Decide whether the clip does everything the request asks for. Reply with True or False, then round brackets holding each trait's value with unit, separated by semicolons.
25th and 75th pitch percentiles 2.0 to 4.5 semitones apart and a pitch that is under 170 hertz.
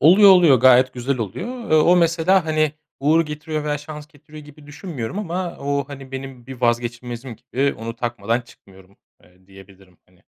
False (4.9 semitones; 140 Hz)